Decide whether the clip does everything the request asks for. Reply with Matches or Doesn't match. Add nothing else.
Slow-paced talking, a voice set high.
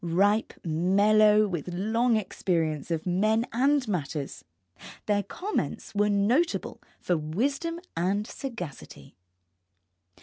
Matches